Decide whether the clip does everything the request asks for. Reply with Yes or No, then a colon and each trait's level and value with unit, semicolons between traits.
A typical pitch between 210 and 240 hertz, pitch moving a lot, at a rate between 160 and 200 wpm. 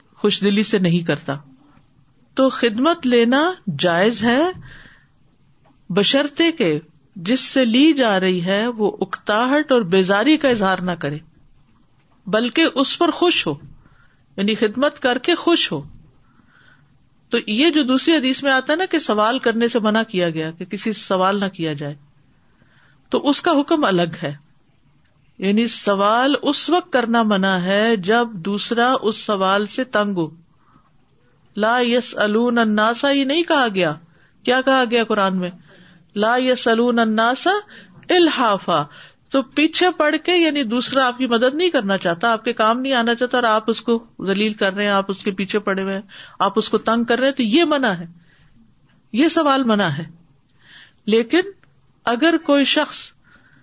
Yes: high, 220 Hz; wide, 6.3 semitones; average, 165 wpm